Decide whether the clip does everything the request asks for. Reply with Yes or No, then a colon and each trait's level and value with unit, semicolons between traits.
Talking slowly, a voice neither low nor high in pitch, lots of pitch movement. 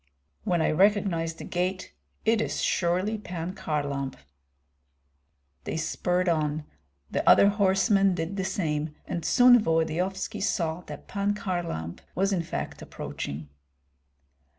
No: slow, 125 wpm; medium, 180 Hz; average, 3.5 semitones